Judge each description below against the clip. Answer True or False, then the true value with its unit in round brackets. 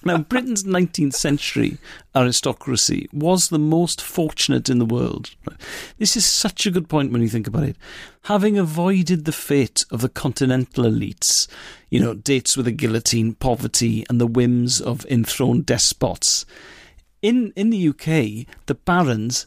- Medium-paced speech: True (155 wpm)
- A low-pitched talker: False (145 Hz)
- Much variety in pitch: True (6.8 semitones)